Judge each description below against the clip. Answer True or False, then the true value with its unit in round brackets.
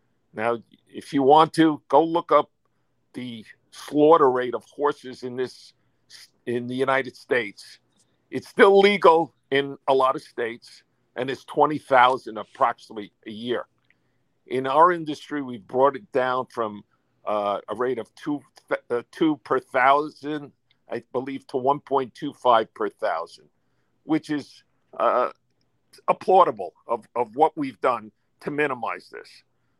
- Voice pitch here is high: False (135 Hz)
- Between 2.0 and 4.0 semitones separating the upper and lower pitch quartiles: True (3.2 semitones)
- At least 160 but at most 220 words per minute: False (145 wpm)